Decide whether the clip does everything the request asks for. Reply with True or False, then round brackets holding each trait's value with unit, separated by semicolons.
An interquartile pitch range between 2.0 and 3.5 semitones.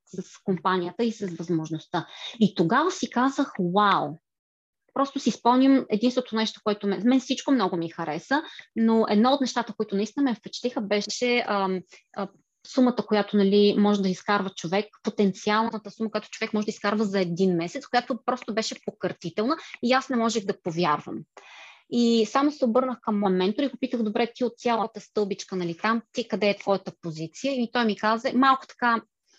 False (4.0 semitones)